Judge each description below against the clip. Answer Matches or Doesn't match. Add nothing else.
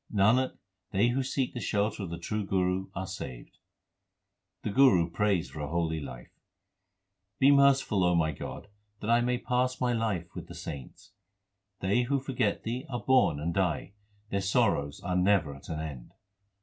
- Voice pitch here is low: Matches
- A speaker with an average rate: Matches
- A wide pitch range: Matches